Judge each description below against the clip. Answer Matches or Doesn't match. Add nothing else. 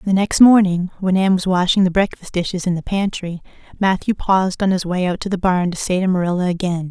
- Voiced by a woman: Matches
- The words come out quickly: Matches